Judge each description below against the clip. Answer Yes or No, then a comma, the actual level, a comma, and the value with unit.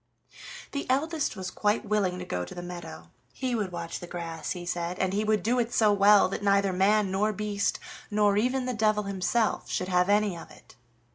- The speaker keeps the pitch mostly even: No, average, 3.0 semitones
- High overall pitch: Yes, high, 200 Hz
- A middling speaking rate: No, fast, 210 wpm